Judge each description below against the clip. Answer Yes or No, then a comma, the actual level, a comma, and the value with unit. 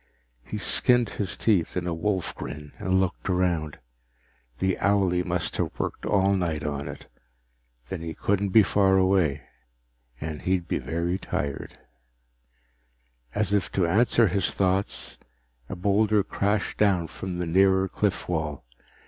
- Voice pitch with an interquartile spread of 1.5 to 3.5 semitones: Yes, average, 2.8 semitones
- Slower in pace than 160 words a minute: Yes, average, 145 wpm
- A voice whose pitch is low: Yes, very low, 95 Hz